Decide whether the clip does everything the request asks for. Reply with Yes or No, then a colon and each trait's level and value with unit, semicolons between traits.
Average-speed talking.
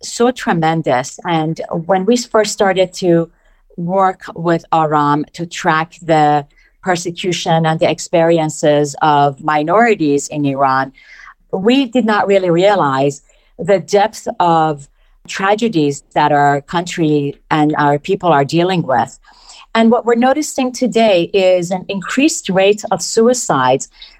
No: slow, 125 wpm